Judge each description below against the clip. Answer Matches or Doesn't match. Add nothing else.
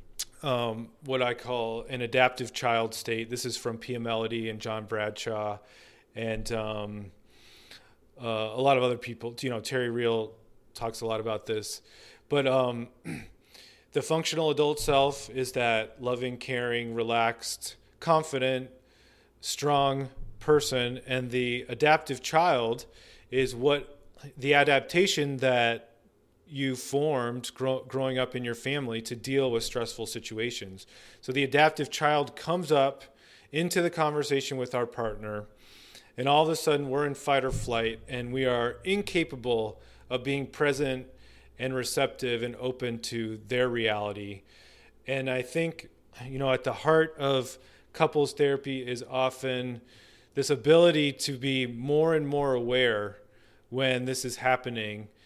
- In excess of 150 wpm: Doesn't match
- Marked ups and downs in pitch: Doesn't match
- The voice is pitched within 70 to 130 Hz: Matches